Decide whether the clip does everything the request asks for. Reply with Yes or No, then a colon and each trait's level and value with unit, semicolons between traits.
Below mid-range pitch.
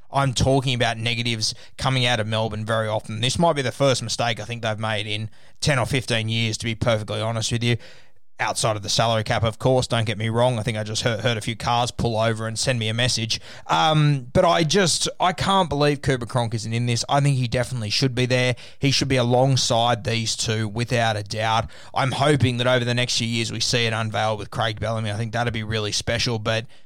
Yes: low, 120 Hz